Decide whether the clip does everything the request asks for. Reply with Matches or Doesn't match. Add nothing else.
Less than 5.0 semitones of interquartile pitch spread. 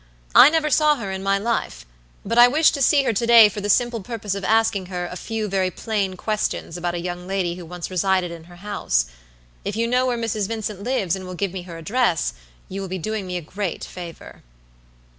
Matches